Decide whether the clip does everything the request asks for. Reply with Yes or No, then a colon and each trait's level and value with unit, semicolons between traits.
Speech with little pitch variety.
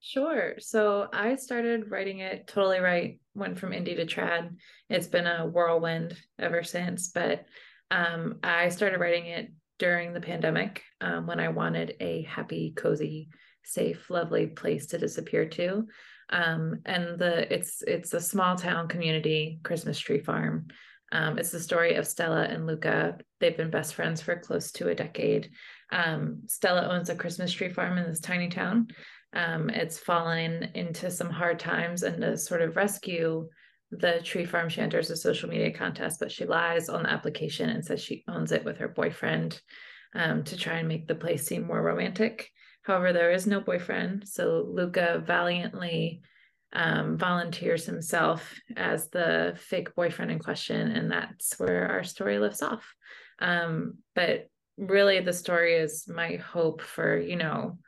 Yes: narrow, 2.3 semitones